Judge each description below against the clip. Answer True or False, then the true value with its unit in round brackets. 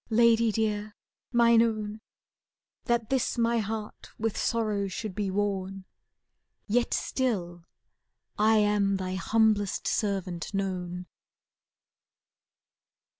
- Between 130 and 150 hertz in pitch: False (210 Hz)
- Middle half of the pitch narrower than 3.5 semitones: True (2.6 semitones)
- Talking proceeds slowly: True (95 wpm)